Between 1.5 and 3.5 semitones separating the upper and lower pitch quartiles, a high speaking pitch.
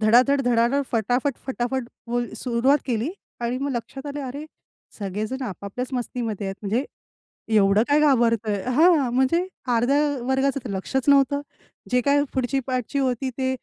Yes: average, 3.0 semitones; very high, 250 Hz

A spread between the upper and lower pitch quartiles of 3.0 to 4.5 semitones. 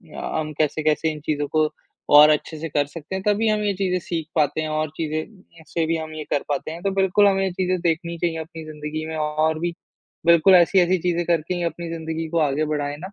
No: narrow, 2.4 semitones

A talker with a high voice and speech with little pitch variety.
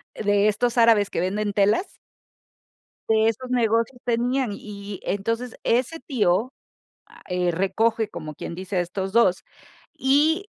No: high, 220 Hz; average, 3.5 semitones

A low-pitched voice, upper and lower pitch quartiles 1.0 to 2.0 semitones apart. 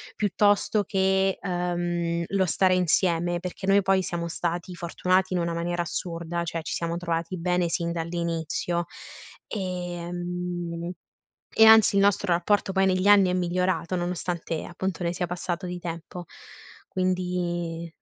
No: medium, 175 Hz; narrow, 1.5 semitones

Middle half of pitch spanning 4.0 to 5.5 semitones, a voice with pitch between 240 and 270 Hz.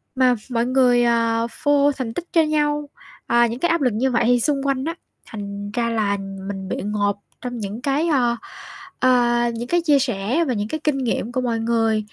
No: average, 3.5 semitones; high, 245 Hz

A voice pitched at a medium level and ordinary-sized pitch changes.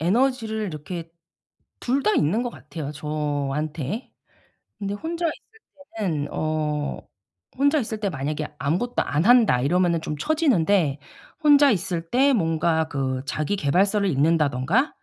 No: medium, 170 Hz; wide, 7.5 semitones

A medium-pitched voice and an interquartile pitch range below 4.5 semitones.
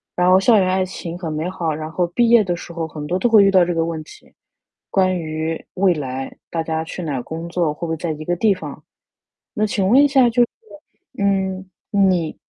Yes: medium, 175 Hz; average, 3.1 semitones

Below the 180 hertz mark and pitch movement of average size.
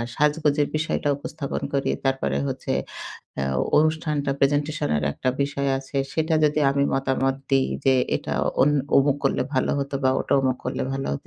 No: medium, 140 Hz; narrow, 1.8 semitones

